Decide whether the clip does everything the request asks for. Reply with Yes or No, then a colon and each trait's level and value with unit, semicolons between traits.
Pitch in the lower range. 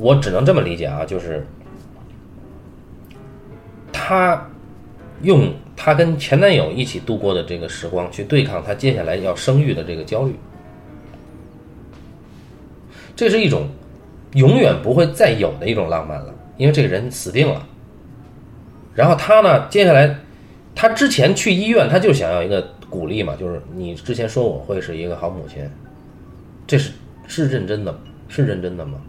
Yes: low, 125 Hz